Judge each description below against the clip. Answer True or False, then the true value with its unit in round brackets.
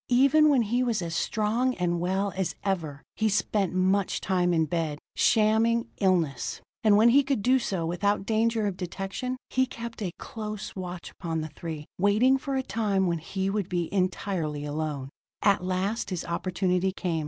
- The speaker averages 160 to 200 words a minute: True (175 wpm)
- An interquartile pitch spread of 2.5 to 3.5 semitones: False (4.3 semitones)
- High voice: True (195 Hz)